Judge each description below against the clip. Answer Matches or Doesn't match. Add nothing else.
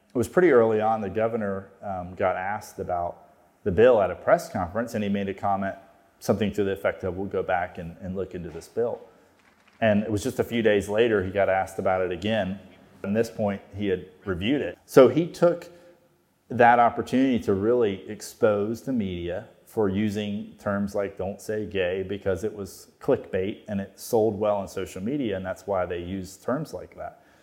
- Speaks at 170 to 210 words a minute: Matches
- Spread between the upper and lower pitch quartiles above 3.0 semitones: Doesn't match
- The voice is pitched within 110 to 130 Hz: Doesn't match